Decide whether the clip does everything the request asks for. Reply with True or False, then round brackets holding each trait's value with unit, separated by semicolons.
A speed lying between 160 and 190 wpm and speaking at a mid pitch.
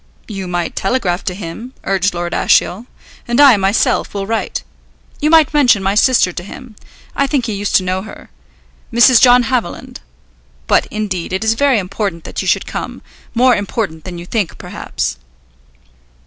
False (170 wpm; 205 Hz)